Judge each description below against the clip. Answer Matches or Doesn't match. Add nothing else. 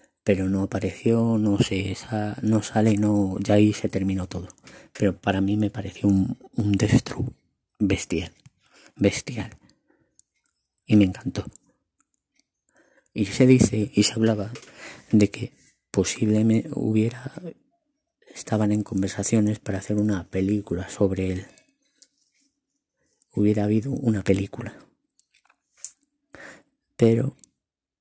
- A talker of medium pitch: Doesn't match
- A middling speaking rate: Doesn't match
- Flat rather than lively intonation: Doesn't match